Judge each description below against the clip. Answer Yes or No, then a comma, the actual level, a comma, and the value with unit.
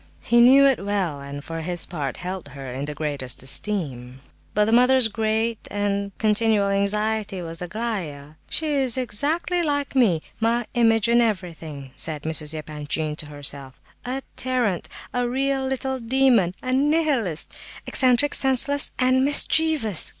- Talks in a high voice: Yes, high, 215 Hz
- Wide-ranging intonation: Yes, wide, 8.3 semitones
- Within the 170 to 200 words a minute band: No, average, 145 wpm